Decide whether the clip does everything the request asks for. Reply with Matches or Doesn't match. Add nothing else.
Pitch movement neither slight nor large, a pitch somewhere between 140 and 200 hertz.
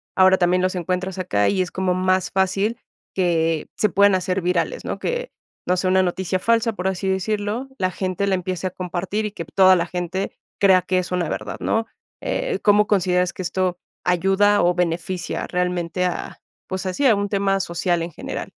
Doesn't match